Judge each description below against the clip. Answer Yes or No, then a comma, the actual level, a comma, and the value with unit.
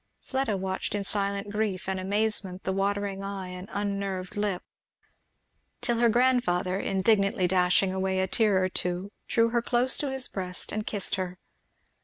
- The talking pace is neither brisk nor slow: Yes, average, 160 wpm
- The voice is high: Yes, high, 195 Hz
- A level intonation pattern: Yes, narrow, 2.3 semitones